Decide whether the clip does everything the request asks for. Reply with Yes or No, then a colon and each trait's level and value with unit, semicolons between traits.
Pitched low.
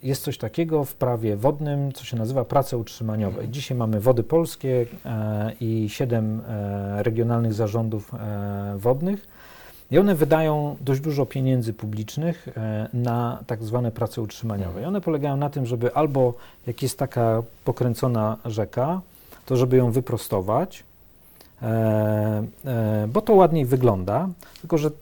Yes: low, 120 Hz